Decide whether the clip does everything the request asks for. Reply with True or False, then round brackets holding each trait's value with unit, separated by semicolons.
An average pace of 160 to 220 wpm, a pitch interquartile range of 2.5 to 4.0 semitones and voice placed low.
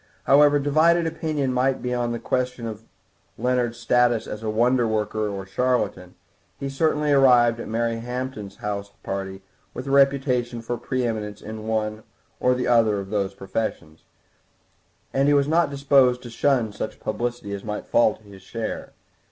True (165 wpm; 3.7 semitones; 120 Hz)